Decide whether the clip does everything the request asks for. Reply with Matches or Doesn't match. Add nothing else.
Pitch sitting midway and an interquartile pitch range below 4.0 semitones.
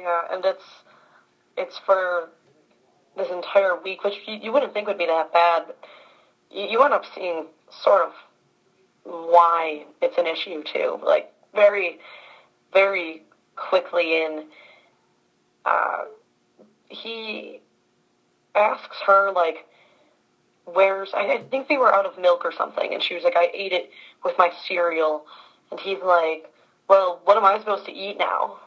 Matches